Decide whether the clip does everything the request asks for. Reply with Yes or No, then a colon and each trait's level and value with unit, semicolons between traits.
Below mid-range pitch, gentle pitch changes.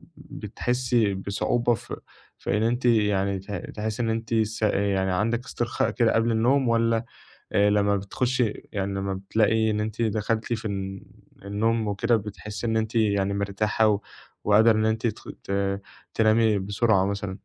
Yes: low, 110 Hz; narrow, 2.2 semitones